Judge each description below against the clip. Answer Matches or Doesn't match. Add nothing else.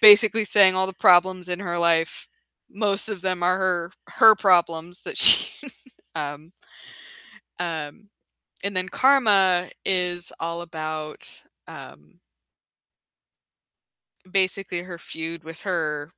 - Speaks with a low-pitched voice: Doesn't match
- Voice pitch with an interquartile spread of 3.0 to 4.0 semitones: Doesn't match